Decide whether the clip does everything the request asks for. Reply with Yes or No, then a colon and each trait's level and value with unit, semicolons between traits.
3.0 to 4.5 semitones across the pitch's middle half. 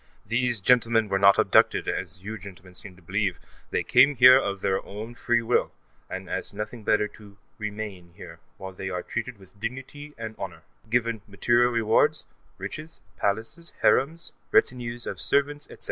Yes: average, 3.8 semitones